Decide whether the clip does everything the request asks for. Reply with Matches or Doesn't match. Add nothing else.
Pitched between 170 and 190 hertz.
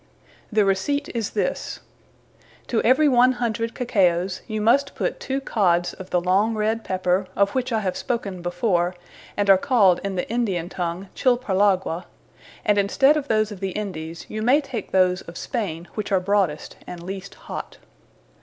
Doesn't match